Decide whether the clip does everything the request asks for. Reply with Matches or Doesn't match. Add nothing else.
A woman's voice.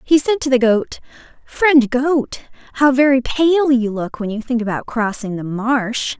Matches